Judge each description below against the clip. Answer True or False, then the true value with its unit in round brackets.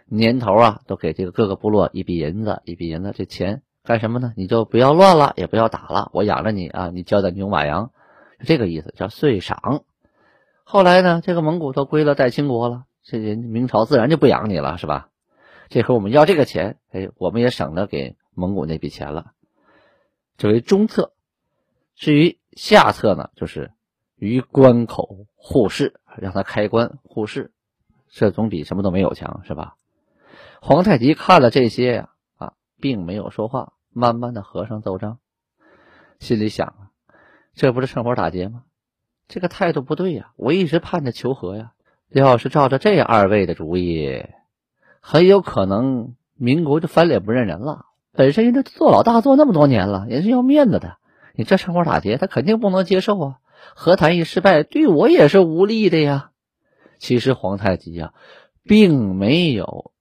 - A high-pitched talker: False (120 Hz)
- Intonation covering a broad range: True (8.2 semitones)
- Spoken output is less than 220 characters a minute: False (265 characters per minute)